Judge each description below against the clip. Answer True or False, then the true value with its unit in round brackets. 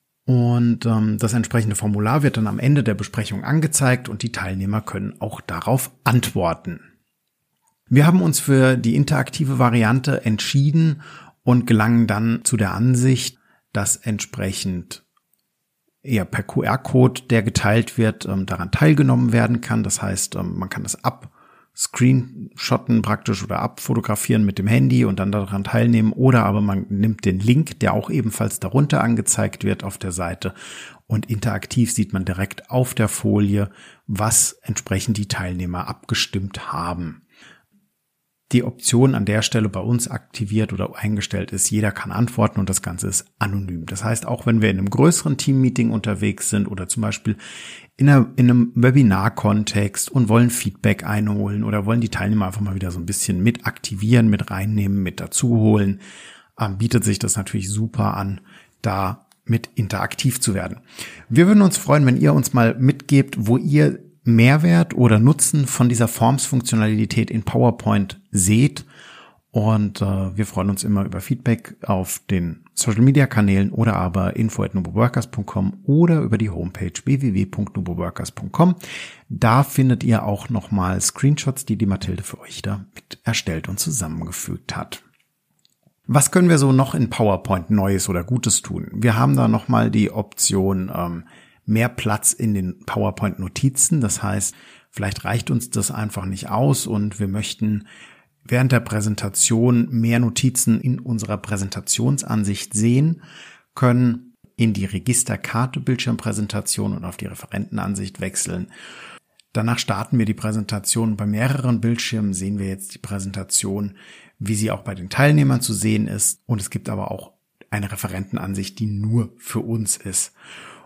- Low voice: True (110 Hz)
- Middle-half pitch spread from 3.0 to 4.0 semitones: True (3.5 semitones)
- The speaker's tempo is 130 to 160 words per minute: True (150 wpm)